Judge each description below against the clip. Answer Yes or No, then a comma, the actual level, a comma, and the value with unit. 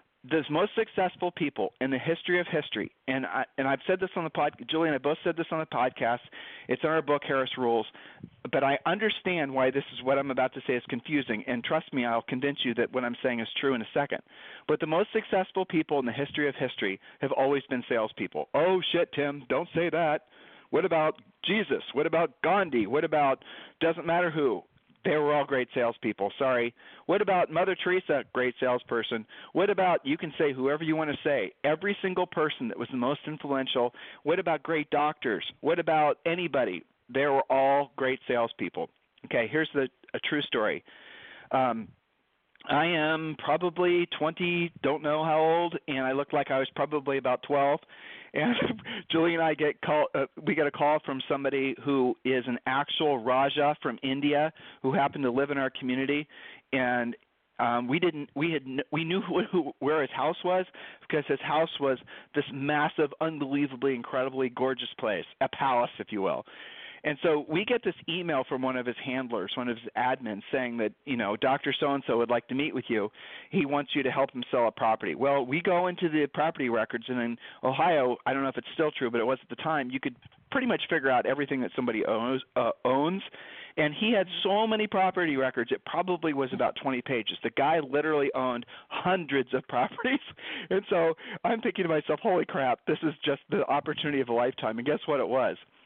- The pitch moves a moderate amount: Yes, average, 3.9 semitones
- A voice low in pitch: No, medium, 145 Hz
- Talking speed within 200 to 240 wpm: Yes, fast, 205 wpm